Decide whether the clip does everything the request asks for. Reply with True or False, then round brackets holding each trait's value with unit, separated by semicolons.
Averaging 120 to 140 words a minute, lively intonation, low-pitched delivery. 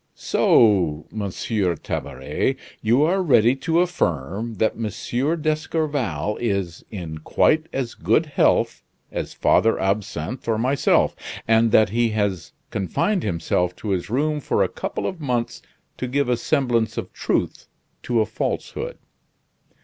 True (135 wpm; 6.0 semitones; 115 Hz)